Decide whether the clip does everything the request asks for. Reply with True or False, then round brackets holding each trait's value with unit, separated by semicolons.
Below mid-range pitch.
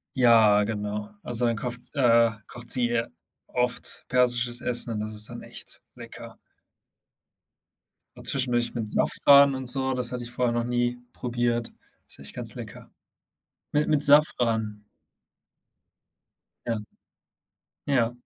True (120 Hz)